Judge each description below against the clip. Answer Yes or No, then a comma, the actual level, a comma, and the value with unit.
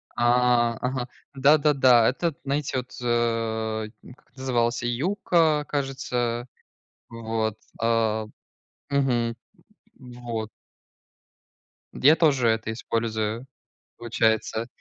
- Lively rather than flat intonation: No, average, 2.8 semitones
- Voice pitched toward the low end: Yes, low, 120 Hz